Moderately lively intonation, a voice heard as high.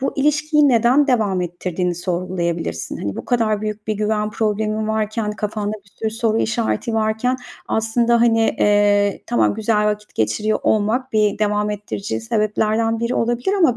No: narrow, 1.9 semitones; high, 215 Hz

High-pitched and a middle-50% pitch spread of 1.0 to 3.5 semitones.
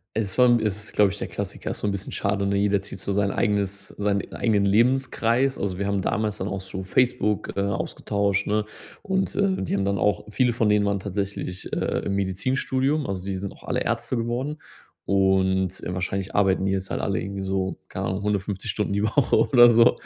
No: low, 100 Hz; narrow, 2.4 semitones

